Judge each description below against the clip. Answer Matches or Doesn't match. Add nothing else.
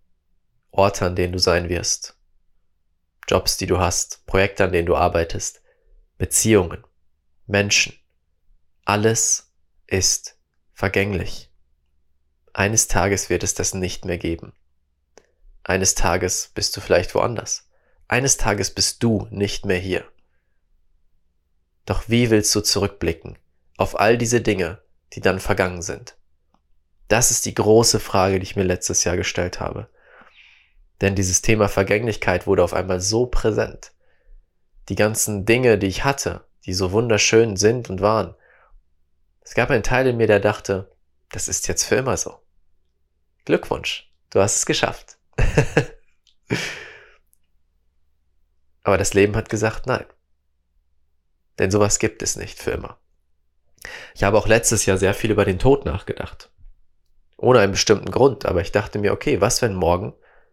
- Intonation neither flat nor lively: Doesn't match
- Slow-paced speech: Doesn't match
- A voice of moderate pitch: Doesn't match